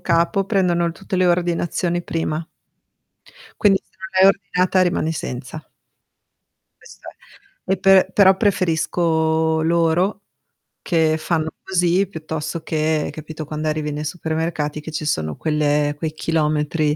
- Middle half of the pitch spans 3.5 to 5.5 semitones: No, narrow, 2.6 semitones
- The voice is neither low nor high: Yes, medium, 160 Hz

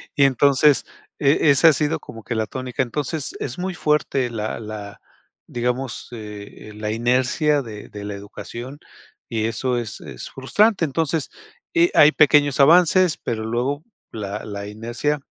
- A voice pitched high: No, low, 130 Hz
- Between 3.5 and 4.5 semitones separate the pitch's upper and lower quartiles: No, average, 5.2 semitones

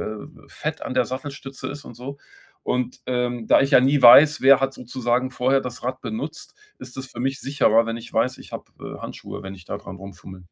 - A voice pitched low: Yes, low, 125 Hz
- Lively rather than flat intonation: No, average, 2.7 semitones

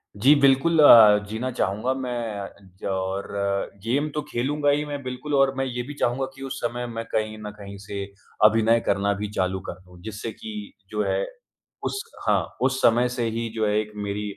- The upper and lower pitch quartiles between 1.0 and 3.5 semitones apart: No, average, 4.4 semitones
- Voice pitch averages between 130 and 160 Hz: No, low, 115 Hz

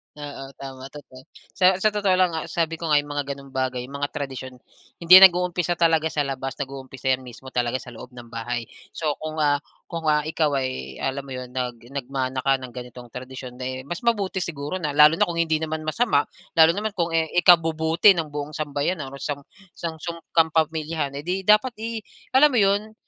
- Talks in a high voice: No, medium, 150 Hz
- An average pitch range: Yes, average, 4.2 semitones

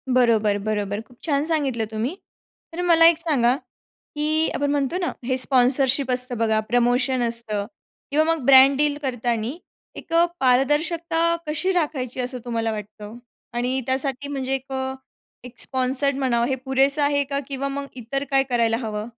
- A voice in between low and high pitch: No, very high, 265 Hz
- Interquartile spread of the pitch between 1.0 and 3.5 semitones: Yes, average, 3.0 semitones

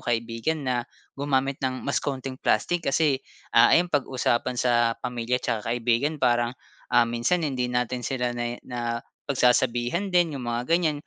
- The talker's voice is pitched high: No, low, 125 Hz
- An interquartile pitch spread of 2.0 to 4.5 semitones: Yes, average, 2.8 semitones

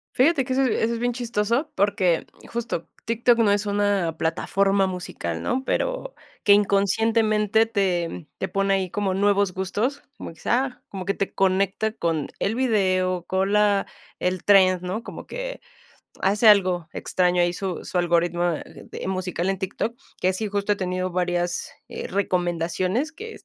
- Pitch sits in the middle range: No, high, 195 Hz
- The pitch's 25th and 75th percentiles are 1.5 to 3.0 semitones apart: No, average, 3.5 semitones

